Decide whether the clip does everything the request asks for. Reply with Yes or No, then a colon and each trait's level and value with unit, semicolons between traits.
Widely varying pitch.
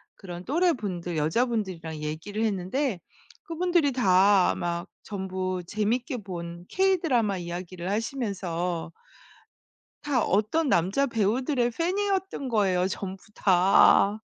Yes: wide, 6.0 semitones